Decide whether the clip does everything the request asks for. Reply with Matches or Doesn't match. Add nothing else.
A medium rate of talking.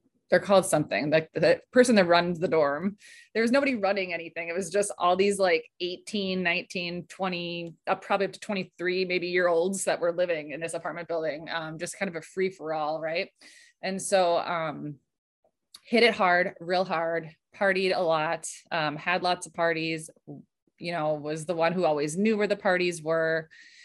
Matches